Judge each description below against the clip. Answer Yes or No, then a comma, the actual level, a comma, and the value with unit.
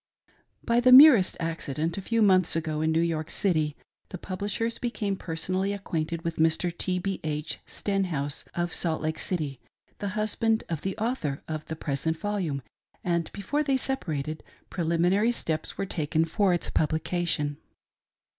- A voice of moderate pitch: Yes, medium, 170 Hz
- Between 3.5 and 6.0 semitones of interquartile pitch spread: Yes, average, 4.2 semitones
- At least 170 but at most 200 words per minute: No, average, 150 wpm